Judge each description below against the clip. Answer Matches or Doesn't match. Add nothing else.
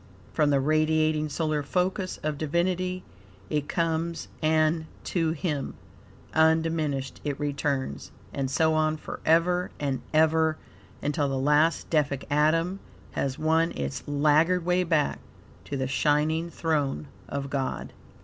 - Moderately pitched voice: Matches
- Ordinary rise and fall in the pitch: Doesn't match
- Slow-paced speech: Matches